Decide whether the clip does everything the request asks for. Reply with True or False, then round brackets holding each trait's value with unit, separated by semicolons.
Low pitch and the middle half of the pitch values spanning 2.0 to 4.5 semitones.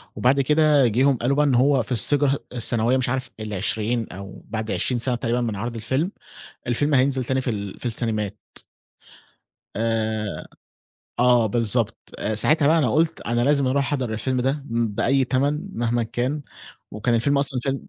True (125 Hz; 3.4 semitones)